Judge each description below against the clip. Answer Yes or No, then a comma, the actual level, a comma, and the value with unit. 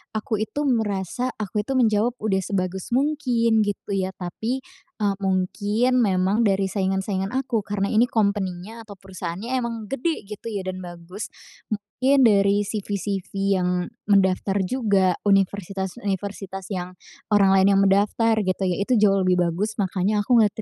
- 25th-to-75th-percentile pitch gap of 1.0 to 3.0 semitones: Yes, narrow, 2.6 semitones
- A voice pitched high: Yes, high, 200 Hz